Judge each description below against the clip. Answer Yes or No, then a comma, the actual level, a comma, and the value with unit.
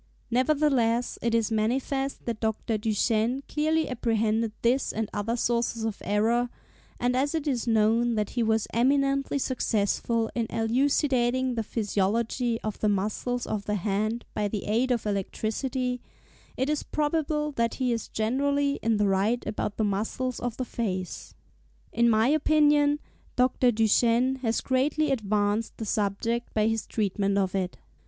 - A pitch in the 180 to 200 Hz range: No, high, 230 Hz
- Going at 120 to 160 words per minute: Yes, average, 150 wpm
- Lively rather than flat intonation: No, average, 3.2 semitones